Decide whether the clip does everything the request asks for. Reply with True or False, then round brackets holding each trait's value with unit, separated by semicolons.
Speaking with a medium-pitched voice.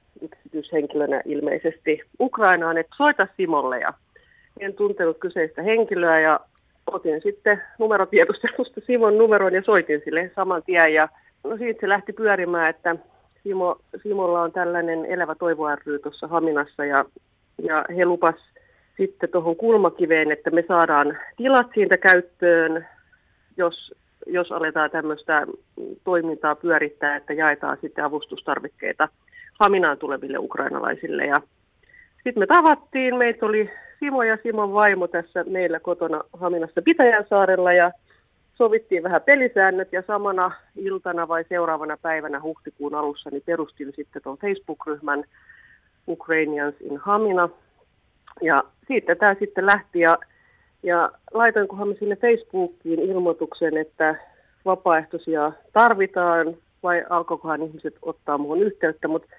True (175 Hz)